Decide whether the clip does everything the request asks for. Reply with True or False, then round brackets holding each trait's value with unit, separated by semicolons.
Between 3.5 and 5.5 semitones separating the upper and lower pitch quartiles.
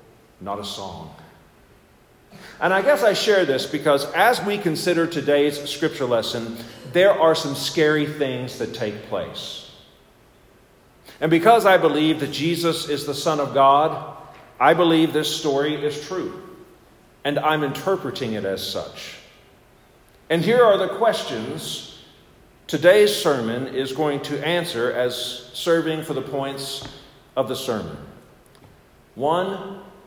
True (3.9 semitones)